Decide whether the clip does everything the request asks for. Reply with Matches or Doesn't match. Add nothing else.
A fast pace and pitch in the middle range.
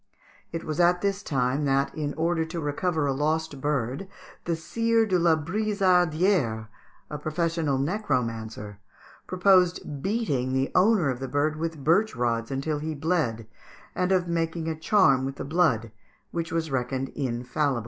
Doesn't match